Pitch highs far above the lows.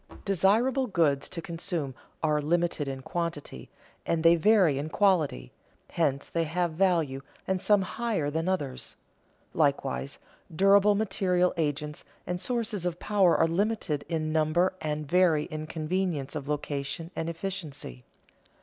No: average, 3.9 semitones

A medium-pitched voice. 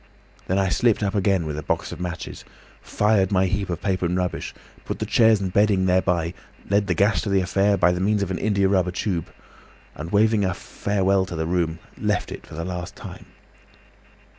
No: very low, 95 Hz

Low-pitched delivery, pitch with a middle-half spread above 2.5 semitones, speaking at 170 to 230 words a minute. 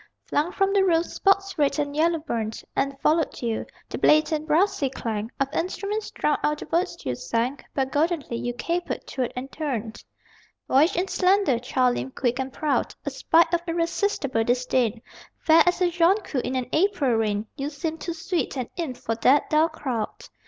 No: very high, 295 Hz; average, 5.2 semitones; average, 180 wpm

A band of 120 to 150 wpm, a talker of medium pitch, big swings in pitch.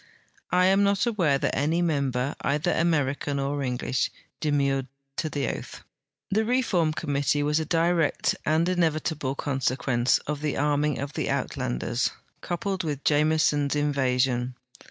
No: average, 140 wpm; medium, 150 Hz; average, 3.2 semitones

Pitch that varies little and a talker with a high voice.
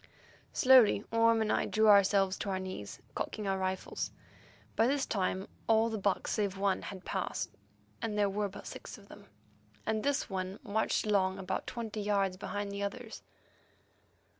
Yes: narrow, 2.3 semitones; high, 205 Hz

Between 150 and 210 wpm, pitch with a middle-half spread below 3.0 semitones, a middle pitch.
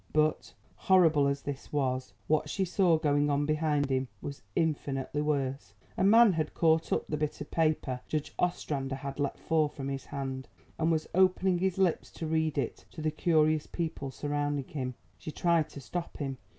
Yes: average, 185 wpm; narrow, 2.6 semitones; medium, 150 Hz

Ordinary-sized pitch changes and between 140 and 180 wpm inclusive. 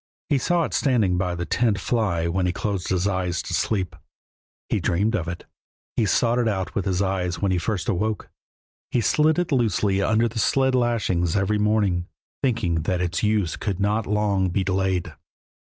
No: average, 3.6 semitones; average, 190 wpm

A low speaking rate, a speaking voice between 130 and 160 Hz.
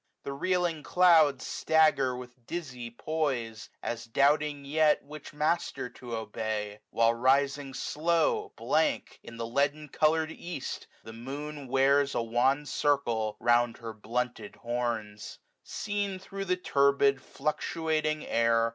Yes: slow, 130 wpm; medium, 140 Hz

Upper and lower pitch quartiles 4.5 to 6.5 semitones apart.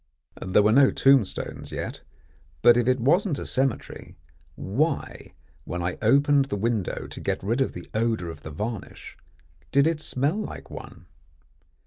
Yes: average, 5.2 semitones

